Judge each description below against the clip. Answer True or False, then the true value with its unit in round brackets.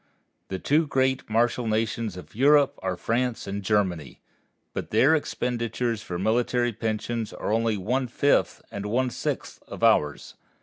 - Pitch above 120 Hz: False (115 Hz)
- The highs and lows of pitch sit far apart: False (3.3 semitones)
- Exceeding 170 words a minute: False (145 wpm)